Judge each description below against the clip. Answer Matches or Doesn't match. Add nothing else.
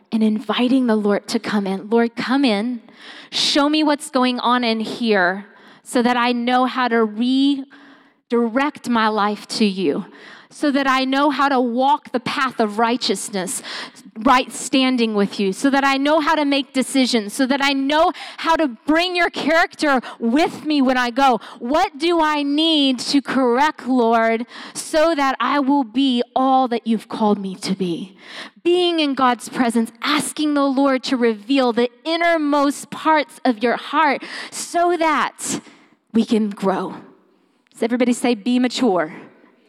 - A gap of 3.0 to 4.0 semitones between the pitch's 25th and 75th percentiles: Matches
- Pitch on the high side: Matches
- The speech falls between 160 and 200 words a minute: Matches